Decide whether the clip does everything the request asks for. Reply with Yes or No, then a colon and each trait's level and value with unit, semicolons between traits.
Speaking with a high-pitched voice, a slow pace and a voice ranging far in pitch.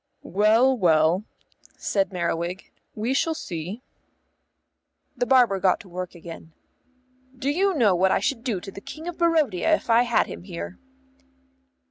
No: high, 210 Hz; average, 150 wpm; wide, 6.5 semitones